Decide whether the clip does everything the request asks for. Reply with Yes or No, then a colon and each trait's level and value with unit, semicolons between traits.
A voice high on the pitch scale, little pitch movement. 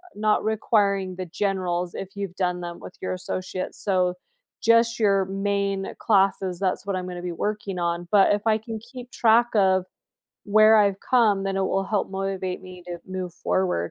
Yes: high, 195 Hz; narrow, 2.3 semitones